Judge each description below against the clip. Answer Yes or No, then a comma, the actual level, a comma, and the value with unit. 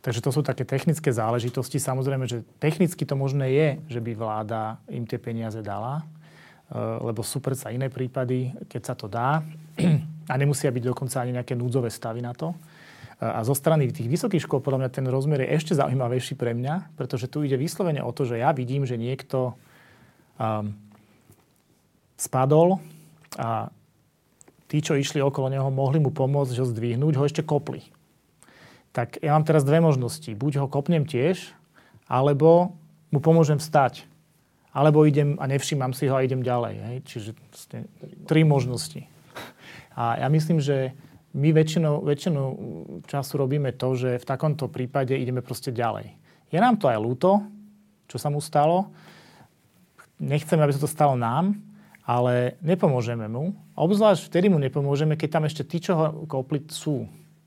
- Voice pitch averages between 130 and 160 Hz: Yes, medium, 140 Hz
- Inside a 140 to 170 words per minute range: Yes, average, 160 wpm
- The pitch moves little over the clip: No, average, 3.8 semitones